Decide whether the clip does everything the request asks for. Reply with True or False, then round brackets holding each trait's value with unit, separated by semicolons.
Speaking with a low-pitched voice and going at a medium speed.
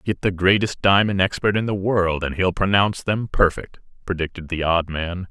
True (95 Hz; 190 wpm)